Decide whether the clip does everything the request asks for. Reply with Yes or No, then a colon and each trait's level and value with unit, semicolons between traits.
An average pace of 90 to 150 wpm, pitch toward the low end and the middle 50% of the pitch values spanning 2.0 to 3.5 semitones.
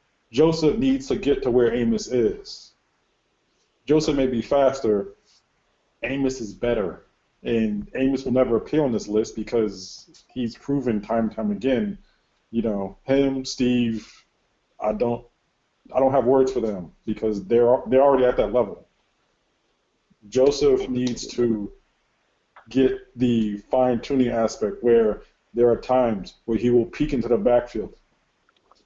Yes: average, 140 wpm; low, 120 Hz; average, 3.0 semitones